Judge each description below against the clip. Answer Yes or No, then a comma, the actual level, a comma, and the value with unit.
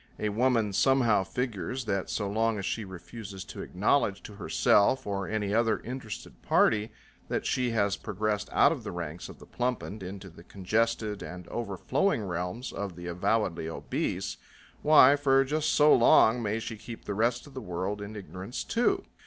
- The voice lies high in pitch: No, low, 105 Hz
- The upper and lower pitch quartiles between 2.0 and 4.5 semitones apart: Yes, average, 3.8 semitones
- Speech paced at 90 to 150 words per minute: No, average, 175 wpm